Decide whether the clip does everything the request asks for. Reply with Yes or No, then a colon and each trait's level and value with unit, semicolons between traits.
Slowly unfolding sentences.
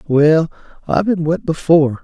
No: average, 145 wpm